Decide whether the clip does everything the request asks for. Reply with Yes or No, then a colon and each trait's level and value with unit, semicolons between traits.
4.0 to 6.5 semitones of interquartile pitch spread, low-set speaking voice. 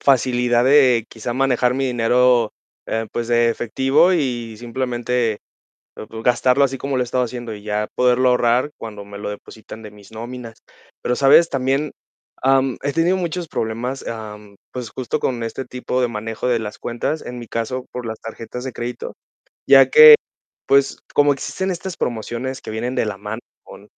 No: average, 2.7 semitones; low, 125 Hz